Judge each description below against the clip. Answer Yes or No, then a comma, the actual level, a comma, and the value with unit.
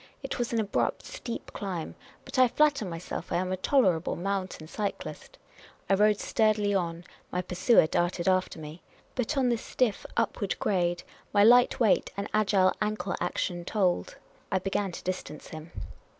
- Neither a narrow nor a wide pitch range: Yes, average, 3.6 semitones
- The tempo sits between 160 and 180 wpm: Yes, average, 165 wpm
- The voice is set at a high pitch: Yes, high, 195 Hz